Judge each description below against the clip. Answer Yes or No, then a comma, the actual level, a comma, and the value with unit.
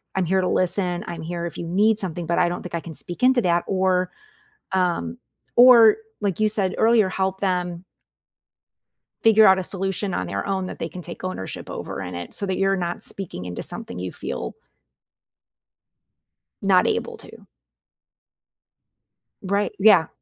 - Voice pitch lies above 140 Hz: Yes, medium, 185 Hz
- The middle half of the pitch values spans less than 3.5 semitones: Yes, narrow, 2.4 semitones